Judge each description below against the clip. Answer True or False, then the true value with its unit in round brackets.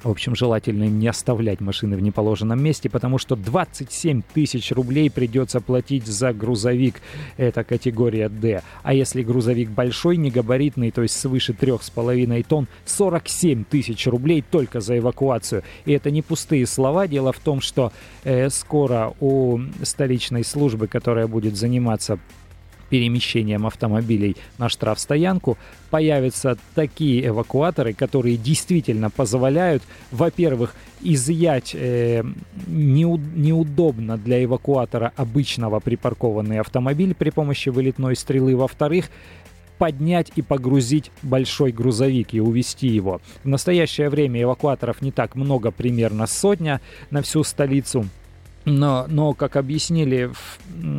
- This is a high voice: False (125 Hz)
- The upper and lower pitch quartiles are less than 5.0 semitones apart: True (3.8 semitones)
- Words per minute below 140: True (125 wpm)